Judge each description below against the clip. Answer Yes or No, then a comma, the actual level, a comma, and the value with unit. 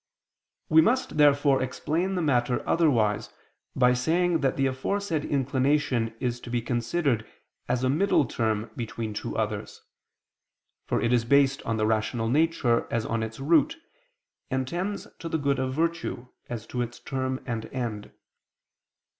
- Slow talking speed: No, average, 155 wpm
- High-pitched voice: No, low, 130 Hz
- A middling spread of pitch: Yes, average, 4.6 semitones